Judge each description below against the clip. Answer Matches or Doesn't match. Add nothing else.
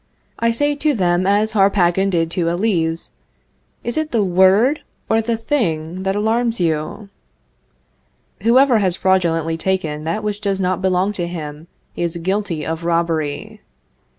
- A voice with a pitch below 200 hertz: Matches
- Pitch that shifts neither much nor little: Matches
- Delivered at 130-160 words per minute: Matches